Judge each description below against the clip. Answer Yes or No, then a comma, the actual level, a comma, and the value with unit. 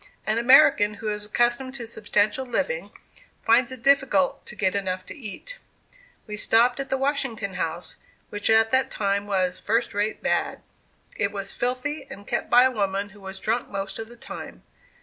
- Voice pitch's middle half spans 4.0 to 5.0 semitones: Yes, average, 4.3 semitones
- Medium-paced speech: Yes, average, 180 wpm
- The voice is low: No, high, 220 Hz